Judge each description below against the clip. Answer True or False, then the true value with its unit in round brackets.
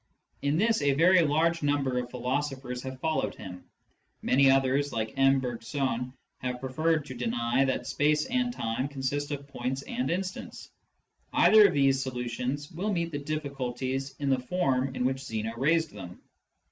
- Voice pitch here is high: False (135 Hz)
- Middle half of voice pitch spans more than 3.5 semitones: False (3.2 semitones)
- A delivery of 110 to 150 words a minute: False (165 wpm)